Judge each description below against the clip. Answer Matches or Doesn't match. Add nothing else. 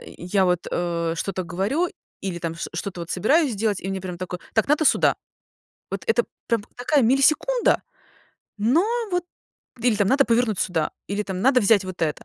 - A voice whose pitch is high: Matches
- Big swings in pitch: Matches